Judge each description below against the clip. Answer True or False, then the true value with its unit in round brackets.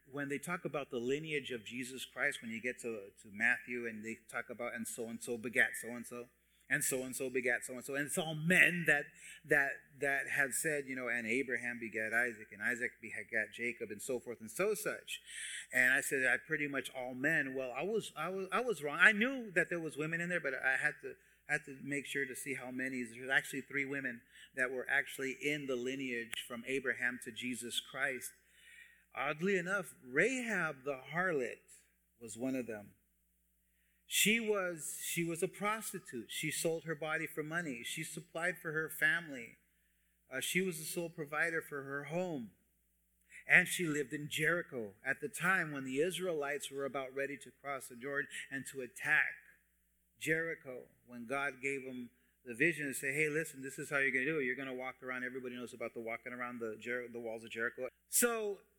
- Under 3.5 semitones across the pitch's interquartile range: False (4.7 semitones)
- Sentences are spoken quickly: True (210 wpm)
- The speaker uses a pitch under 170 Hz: True (135 Hz)